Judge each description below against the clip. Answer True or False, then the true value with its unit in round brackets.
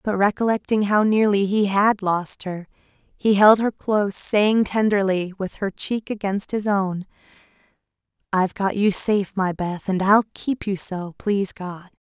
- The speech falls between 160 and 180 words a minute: True (165 wpm)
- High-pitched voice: True (200 Hz)